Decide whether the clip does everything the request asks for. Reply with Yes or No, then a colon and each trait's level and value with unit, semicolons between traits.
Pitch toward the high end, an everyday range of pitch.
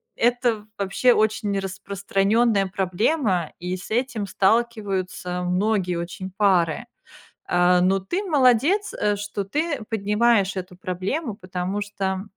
Yes: high, 200 Hz; average, 3.8 semitones